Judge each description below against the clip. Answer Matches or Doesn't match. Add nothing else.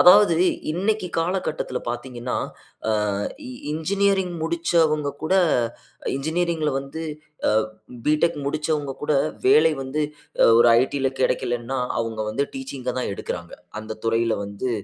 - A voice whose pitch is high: Doesn't match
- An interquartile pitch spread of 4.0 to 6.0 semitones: Matches